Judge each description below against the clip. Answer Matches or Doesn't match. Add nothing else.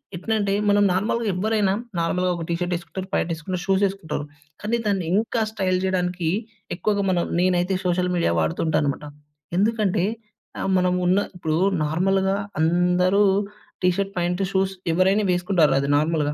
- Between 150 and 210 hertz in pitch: Matches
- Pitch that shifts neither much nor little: Doesn't match